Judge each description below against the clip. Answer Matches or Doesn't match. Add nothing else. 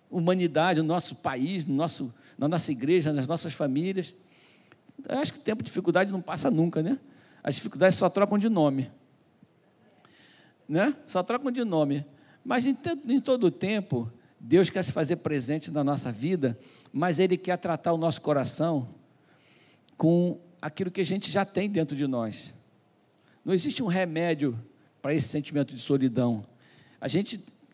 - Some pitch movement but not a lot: Matches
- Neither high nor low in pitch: Matches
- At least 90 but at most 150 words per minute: Doesn't match